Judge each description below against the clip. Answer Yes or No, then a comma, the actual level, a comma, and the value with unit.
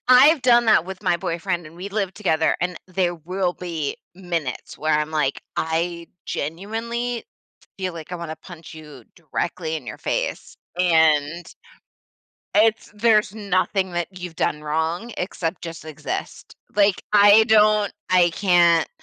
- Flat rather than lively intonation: No, average, 4.0 semitones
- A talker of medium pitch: Yes, medium, 175 Hz